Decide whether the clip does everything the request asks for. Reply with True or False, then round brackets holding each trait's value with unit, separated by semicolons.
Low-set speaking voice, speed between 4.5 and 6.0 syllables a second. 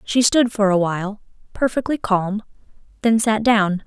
False (215 Hz; 4.6 syllables/s)